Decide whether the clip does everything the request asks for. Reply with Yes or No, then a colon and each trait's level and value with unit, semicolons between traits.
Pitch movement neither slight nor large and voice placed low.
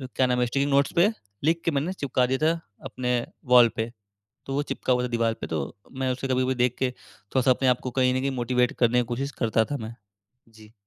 No: narrow, 2.1 semitones; low, 125 Hz